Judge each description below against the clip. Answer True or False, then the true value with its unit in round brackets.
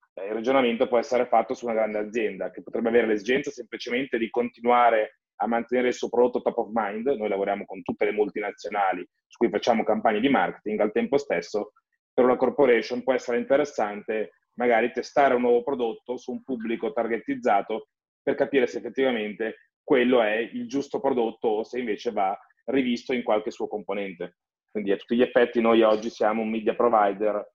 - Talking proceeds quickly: True (180 wpm)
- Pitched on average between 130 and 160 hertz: False (120 Hz)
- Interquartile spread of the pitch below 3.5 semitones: True (2.7 semitones)